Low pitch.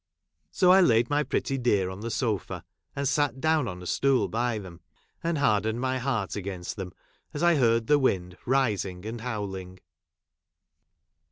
Yes: low, 115 Hz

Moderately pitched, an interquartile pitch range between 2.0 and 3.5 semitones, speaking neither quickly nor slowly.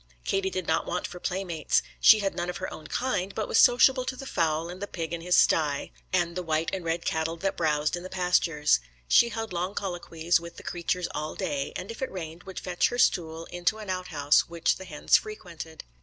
No: medium, 175 Hz; average, 2.7 semitones; fast, 230 wpm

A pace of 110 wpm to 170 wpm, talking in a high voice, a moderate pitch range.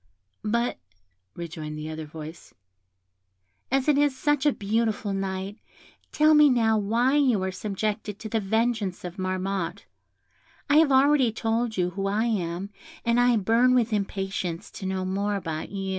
Yes: average, 160 wpm; high, 210 Hz; average, 4.2 semitones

